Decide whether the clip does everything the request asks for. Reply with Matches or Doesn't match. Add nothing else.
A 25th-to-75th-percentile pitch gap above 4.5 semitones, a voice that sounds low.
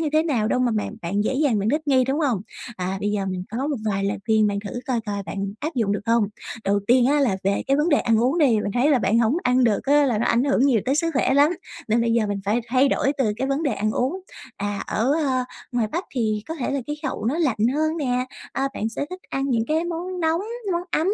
Doesn't match